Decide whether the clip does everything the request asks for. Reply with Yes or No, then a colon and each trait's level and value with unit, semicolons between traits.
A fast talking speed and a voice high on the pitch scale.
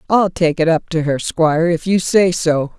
No: fast, 235 wpm; medium, 170 Hz